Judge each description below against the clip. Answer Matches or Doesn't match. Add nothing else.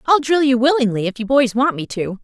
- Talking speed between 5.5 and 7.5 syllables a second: Matches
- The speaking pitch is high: Matches